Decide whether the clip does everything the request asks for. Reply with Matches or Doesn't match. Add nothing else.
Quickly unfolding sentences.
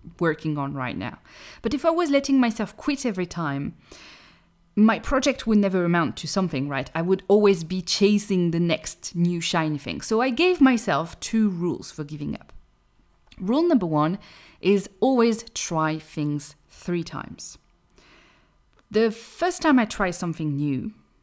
Doesn't match